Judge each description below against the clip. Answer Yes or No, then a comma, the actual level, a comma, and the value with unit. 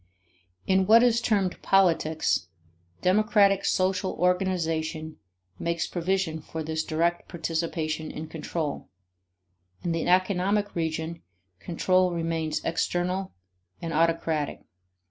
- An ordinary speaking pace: No, slow, 100 wpm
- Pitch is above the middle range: No, medium, 170 Hz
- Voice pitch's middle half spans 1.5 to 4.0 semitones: Yes, average, 2.8 semitones